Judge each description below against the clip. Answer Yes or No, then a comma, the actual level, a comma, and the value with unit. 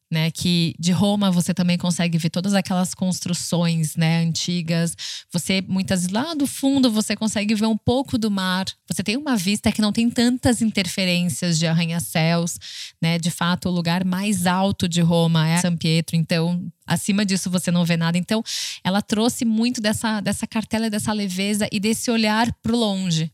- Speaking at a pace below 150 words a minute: No, average, 180 wpm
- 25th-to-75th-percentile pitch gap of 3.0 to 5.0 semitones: Yes, average, 4.0 semitones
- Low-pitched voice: No, medium, 185 Hz